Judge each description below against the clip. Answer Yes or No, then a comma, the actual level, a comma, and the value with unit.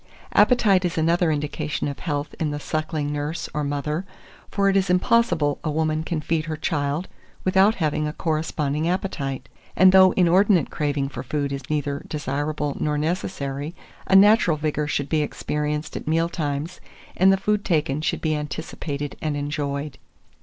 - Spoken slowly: No, average, 165 wpm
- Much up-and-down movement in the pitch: No, average, 3.1 semitones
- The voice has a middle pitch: Yes, medium, 155 Hz